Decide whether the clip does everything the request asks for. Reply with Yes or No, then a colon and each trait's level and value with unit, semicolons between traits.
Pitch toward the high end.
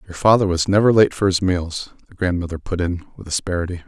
No: very low, 90 Hz